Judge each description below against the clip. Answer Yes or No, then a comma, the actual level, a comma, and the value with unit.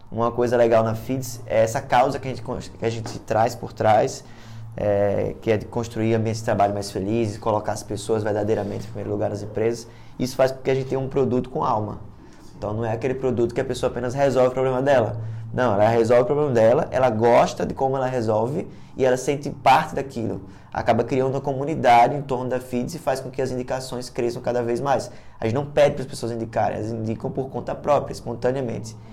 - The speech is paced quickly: Yes, fast, 225 wpm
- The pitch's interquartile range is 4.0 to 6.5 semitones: No, average, 2.7 semitones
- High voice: No, low, 120 Hz